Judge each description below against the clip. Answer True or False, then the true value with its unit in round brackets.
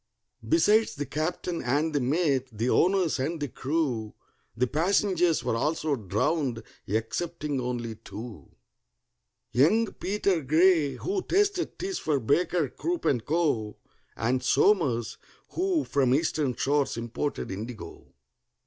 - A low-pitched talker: False (145 Hz)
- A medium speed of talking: False (120 wpm)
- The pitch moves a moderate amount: False (6.1 semitones)